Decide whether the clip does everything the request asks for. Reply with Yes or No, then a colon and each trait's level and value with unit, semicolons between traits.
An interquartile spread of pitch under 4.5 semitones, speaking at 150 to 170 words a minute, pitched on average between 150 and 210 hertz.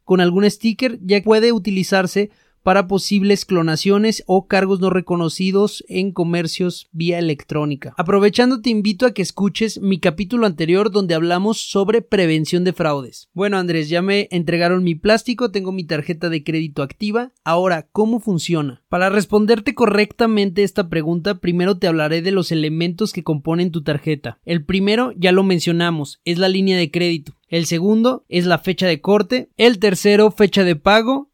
Yes: average, 3.4 semitones; average, 165 wpm; high, 190 Hz